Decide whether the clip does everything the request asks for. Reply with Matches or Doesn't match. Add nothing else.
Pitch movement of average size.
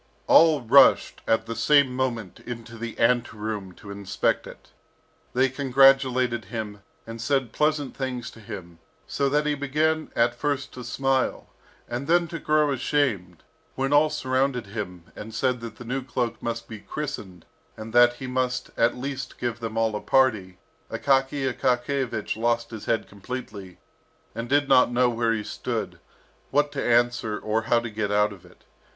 Matches